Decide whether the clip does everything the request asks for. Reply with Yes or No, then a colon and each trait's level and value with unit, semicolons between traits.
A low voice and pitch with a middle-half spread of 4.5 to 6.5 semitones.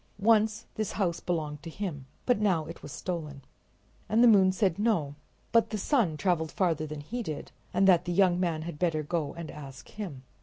No: medium, 175 Hz; average, 4.8 semitones